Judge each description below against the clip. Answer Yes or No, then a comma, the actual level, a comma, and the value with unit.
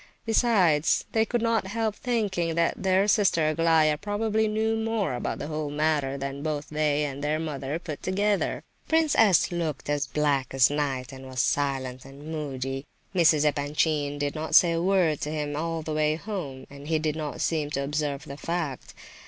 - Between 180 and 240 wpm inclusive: Yes, average, 185 wpm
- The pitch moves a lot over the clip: No, average, 4.4 semitones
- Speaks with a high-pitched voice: No, medium, 155 Hz